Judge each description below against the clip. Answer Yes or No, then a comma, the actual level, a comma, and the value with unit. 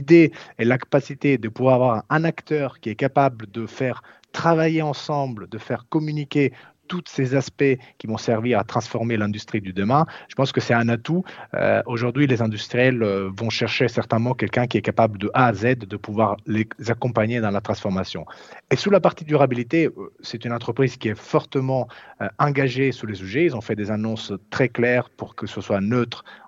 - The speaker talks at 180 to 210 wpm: Yes, average, 195 wpm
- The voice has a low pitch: Yes, low, 120 Hz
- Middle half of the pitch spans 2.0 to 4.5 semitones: Yes, average, 3.7 semitones